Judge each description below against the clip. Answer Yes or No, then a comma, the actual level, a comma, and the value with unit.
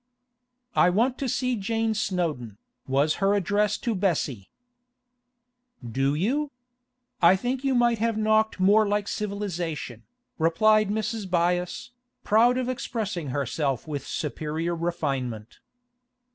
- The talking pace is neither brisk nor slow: No, slow, 120 wpm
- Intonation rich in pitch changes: Yes, wide, 5.8 semitones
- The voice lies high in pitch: Yes, high, 195 Hz